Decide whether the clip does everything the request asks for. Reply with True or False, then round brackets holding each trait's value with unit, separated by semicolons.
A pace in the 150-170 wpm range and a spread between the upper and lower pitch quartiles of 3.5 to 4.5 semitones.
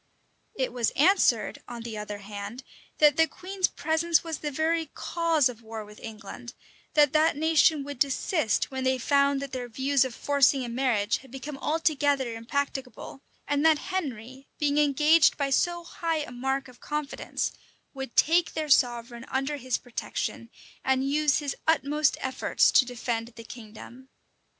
True (160 wpm; 3.8 semitones)